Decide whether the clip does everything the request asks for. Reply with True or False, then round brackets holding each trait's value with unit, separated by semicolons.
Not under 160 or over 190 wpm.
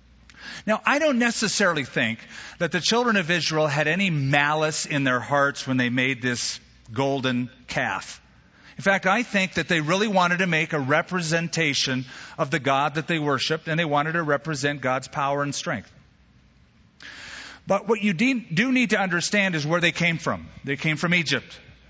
True (180 wpm)